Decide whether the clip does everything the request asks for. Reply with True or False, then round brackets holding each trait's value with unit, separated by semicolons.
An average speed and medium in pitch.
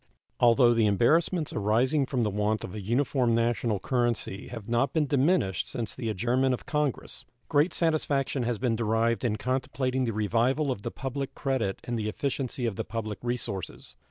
False (175 wpm; 120 Hz)